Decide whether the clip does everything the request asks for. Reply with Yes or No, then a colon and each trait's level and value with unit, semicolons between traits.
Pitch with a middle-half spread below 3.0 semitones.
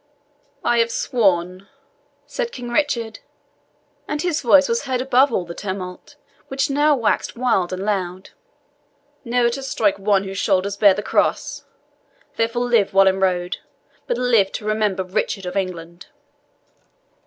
No: average, 4.6 semitones